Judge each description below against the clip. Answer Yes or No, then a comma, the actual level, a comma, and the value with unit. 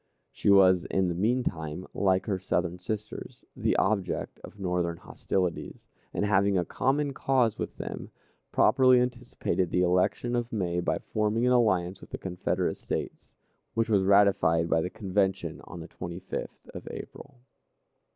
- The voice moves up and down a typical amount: Yes, average, 4.0 semitones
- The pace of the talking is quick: No, average, 155 wpm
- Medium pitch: No, very low, 95 Hz